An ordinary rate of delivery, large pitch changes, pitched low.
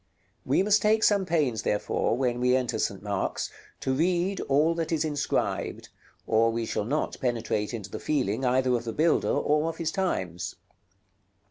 Yes: average, 170 wpm; wide, 6.2 semitones; low, 130 Hz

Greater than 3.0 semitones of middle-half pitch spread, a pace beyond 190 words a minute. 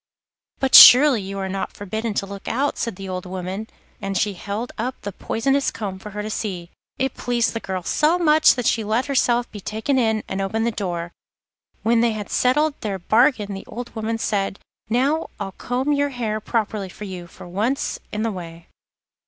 Yes: average, 4.0 semitones; average, 200 wpm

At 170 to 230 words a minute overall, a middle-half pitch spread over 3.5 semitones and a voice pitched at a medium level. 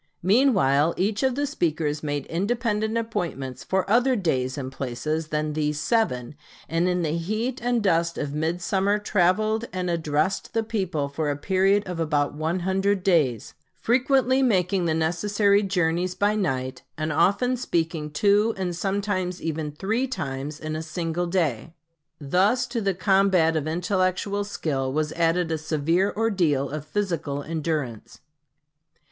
No: average, 150 wpm; average, 4.8 semitones; medium, 175 Hz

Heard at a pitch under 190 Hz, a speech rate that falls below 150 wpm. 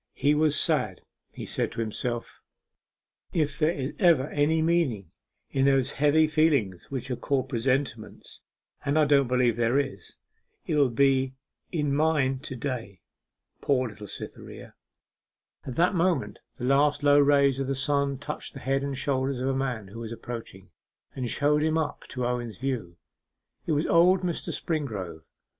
No: low, 135 Hz; average, 165 wpm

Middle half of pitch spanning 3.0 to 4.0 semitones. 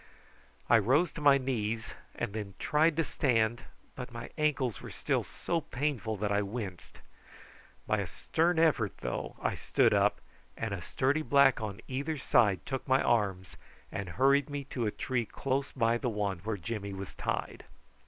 No: average, 5.0 semitones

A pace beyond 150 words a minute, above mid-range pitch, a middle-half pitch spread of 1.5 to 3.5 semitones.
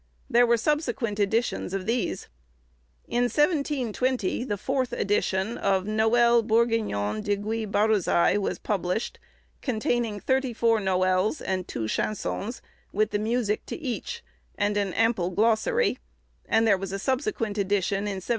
No: average, 140 wpm; high, 220 Hz; average, 3.2 semitones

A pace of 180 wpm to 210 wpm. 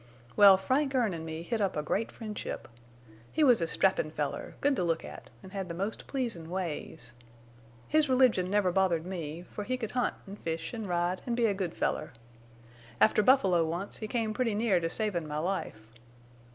Yes: average, 195 wpm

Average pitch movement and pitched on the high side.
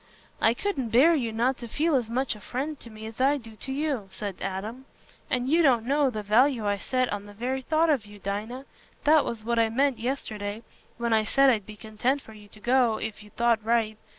Yes: average, 3.7 semitones; high, 235 Hz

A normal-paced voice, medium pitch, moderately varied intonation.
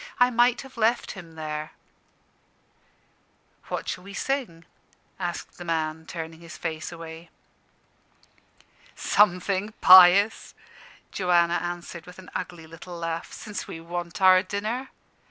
No: slow, 120 wpm; medium, 175 Hz; average, 3.4 semitones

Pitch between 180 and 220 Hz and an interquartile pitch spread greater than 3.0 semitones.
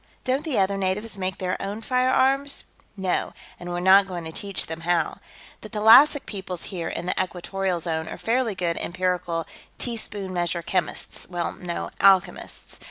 Yes: high, 190 Hz; average, 3.4 semitones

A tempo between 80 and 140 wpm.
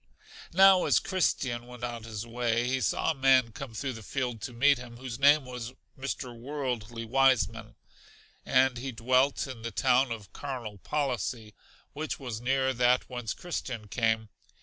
No: average, 165 wpm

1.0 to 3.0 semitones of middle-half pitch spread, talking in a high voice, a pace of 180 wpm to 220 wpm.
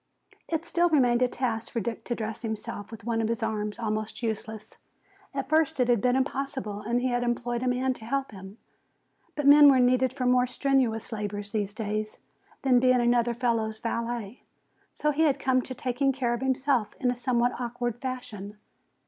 Yes: average, 2.7 semitones; high, 240 Hz; average, 190 wpm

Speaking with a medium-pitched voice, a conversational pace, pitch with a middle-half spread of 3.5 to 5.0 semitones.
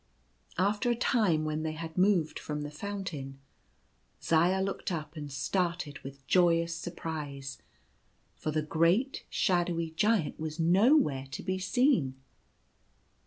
No: medium, 165 Hz; slow, 125 wpm; average, 3.9 semitones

